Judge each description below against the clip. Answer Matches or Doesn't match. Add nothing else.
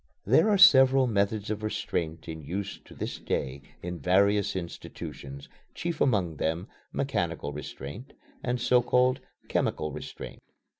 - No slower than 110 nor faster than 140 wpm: Matches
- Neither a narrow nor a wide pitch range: Doesn't match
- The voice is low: Matches